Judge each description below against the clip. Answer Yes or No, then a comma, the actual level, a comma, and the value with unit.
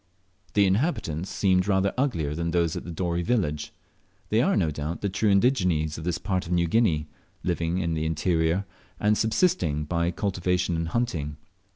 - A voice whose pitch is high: No, very low, 90 Hz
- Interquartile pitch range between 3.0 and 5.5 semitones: Yes, average, 3.5 semitones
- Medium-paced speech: Yes, average, 170 wpm